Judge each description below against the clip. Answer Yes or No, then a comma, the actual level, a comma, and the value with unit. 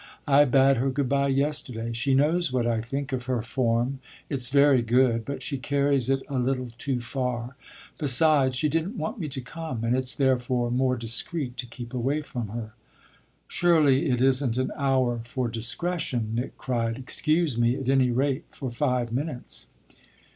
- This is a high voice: No, low, 130 Hz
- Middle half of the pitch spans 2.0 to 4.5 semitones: Yes, narrow, 2.6 semitones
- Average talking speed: Yes, average, 175 wpm